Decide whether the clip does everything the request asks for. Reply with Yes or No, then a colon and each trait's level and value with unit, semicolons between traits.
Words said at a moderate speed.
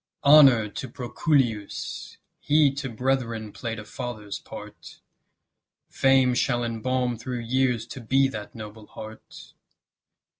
No: slow, 115 wpm